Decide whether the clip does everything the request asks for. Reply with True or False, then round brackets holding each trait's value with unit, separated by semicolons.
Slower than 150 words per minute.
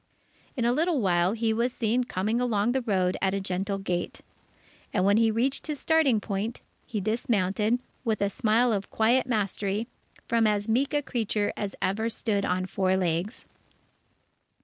False (170 wpm)